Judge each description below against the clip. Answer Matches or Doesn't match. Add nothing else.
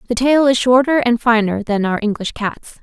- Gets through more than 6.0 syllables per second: Doesn't match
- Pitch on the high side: Matches